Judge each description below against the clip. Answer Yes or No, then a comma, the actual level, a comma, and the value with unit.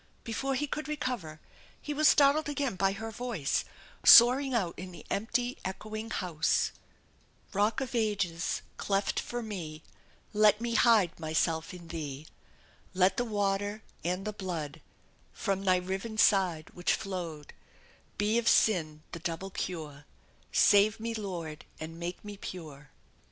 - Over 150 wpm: No, average, 140 wpm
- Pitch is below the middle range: No, high, 195 Hz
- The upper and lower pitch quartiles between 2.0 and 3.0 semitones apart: No, average, 5.1 semitones